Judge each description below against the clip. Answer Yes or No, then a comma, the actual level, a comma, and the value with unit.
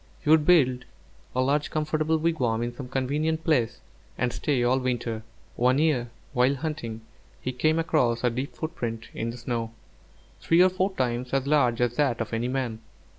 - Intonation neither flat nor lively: Yes, average, 4.3 semitones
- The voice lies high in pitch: No, low, 130 Hz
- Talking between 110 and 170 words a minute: No, average, 180 wpm